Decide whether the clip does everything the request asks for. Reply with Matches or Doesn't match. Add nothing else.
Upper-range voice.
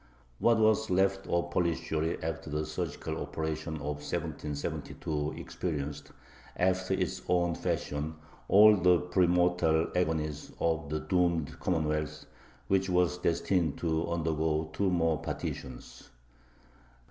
Doesn't match